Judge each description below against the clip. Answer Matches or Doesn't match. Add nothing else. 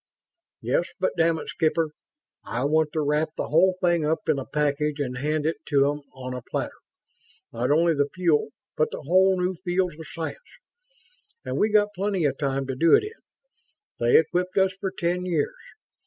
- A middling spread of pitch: Matches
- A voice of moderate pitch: Matches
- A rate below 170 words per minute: Doesn't match